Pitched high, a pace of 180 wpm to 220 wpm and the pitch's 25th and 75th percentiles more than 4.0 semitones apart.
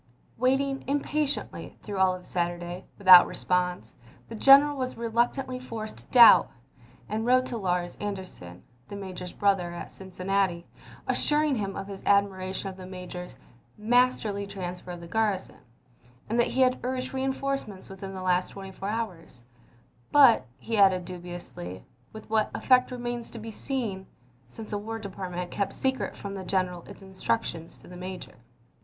No: high, 195 Hz; average, 165 wpm; average, 4.5 semitones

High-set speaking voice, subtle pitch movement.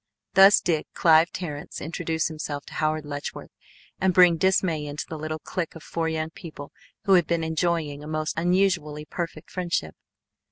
No: medium, 160 Hz; narrow, 2.2 semitones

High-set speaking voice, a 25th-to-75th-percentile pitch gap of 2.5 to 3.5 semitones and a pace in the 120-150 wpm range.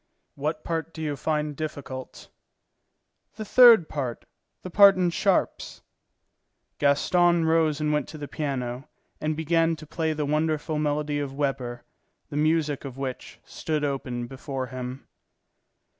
No: medium, 150 Hz; average, 2.8 semitones; average, 140 wpm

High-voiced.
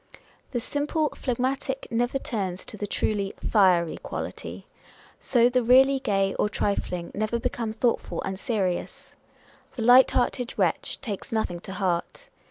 Yes: high, 225 Hz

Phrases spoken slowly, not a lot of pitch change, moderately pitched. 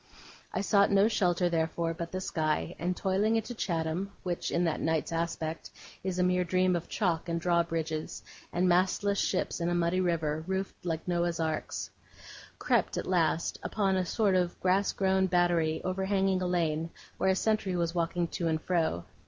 No: average, 175 wpm; narrow, 2.2 semitones; medium, 175 Hz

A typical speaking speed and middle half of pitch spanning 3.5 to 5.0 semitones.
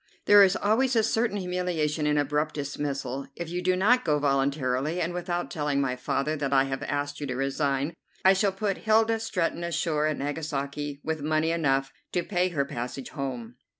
Yes: average, 185 wpm; average, 4.6 semitones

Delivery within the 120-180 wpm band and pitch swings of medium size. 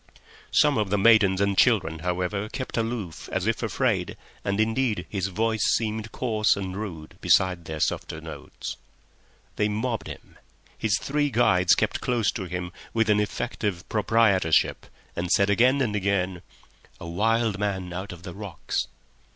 Yes: average, 160 wpm; average, 3.6 semitones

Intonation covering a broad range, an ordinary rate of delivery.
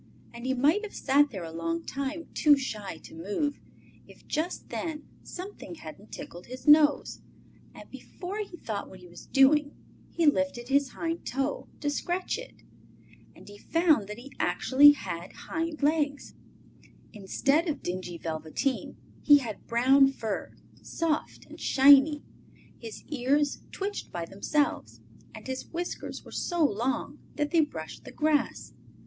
Yes: wide, 6.0 semitones; average, 150 wpm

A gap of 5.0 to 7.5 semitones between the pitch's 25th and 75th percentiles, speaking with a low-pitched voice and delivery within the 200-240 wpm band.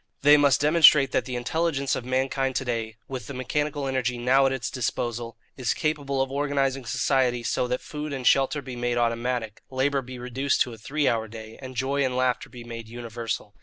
No: narrow, 2.4 semitones; low, 130 Hz; fast, 205 wpm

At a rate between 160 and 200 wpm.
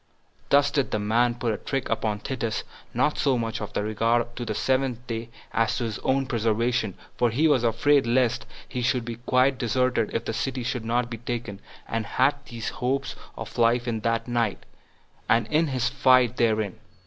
Yes: average, 190 wpm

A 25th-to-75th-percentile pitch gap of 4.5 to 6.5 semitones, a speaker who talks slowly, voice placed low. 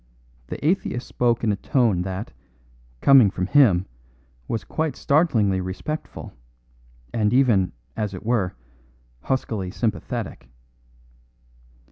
Yes: average, 5.2 semitones; slow, 105 wpm; low, 110 Hz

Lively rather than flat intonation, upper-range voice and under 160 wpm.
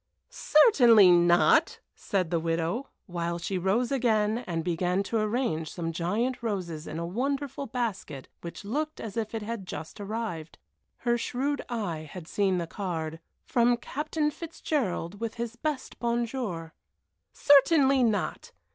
Yes: wide, 6.0 semitones; high, 210 Hz; average, 140 wpm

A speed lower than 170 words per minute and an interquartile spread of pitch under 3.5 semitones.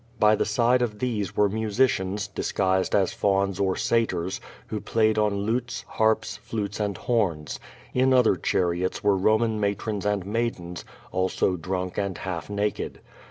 Yes: average, 155 wpm; average, 2.8 semitones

